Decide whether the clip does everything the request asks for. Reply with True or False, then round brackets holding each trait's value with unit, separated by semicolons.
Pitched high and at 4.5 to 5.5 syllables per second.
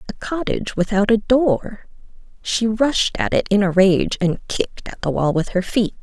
True (205 Hz; 4.7 syllables/s)